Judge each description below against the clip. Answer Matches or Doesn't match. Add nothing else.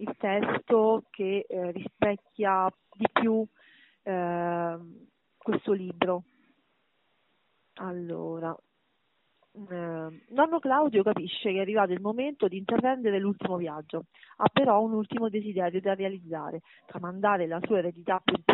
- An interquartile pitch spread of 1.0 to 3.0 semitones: Doesn't match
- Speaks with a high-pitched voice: Matches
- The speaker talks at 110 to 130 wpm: Matches